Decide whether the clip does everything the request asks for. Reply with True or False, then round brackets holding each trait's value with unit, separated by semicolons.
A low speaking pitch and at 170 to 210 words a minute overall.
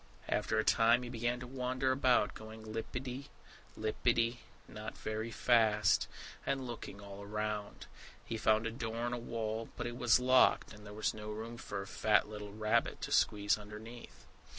True (115 Hz; 175 wpm)